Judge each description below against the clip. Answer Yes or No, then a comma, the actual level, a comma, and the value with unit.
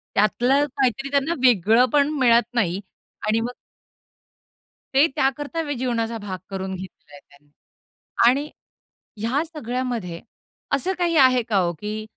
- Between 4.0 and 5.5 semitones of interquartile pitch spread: Yes, average, 4.9 semitones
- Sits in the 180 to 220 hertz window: No, high, 240 Hz